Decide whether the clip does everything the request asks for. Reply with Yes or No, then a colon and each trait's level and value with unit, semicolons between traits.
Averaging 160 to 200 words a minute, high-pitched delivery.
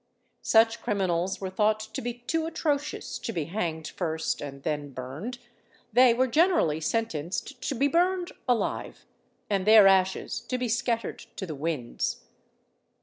No: average, 145 wpm; high, 215 Hz